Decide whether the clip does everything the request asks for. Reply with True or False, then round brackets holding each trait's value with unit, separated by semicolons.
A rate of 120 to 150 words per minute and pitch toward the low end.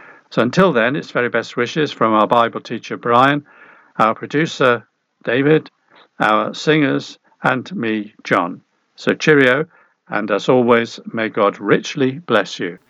True (140 wpm; 120 Hz)